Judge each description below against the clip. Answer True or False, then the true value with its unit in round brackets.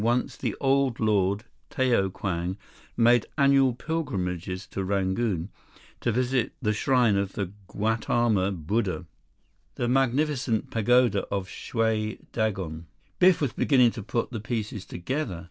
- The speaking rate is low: True (130 wpm)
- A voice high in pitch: False (110 Hz)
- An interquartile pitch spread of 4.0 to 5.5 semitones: True (4.4 semitones)